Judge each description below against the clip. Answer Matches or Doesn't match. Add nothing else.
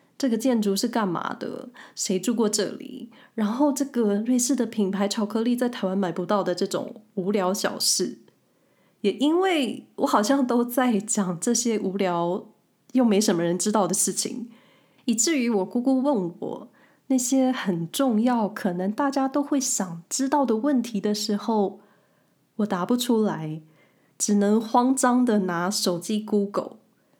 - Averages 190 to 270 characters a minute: Matches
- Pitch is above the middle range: Matches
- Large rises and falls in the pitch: Doesn't match